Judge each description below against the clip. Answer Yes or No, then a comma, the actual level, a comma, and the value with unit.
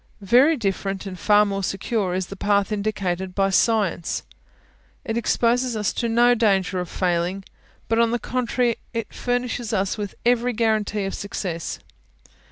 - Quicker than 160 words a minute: No, average, 155 wpm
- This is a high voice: Yes, high, 210 Hz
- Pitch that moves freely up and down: No, average, 3.3 semitones